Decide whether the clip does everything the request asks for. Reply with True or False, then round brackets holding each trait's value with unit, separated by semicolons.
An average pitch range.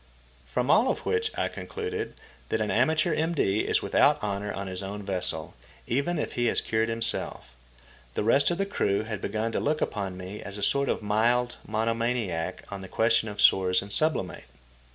False (5.7 semitones)